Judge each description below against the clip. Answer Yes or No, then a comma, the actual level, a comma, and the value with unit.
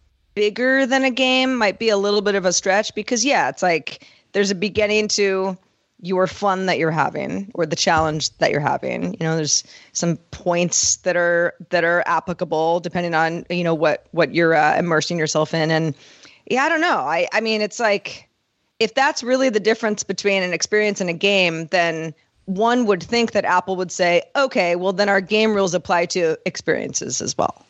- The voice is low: No, high, 190 Hz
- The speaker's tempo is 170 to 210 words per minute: Yes, average, 200 wpm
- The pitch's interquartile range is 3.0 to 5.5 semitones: Yes, average, 3.9 semitones